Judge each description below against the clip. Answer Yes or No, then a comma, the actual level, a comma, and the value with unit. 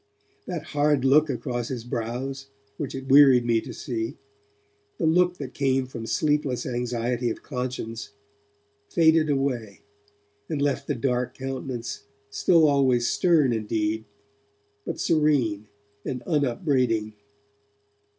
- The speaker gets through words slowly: Yes, slow, 120 wpm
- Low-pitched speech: Yes, low, 130 Hz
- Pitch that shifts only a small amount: No, average, 3.4 semitones